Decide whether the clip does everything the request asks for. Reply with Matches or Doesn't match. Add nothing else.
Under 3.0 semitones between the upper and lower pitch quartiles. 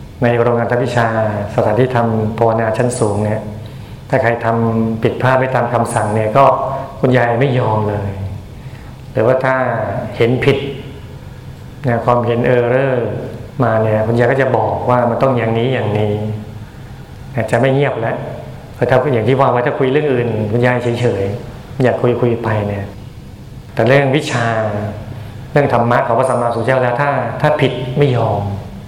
Matches